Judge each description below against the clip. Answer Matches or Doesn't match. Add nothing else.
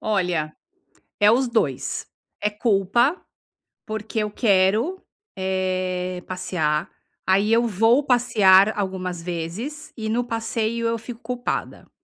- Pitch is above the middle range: Matches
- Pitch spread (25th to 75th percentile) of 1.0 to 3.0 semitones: Doesn't match